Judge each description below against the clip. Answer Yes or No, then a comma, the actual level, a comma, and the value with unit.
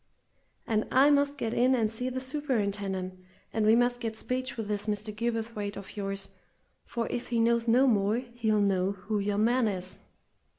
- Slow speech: No, average, 180 wpm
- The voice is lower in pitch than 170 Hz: No, high, 225 Hz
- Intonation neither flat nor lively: Yes, average, 3.1 semitones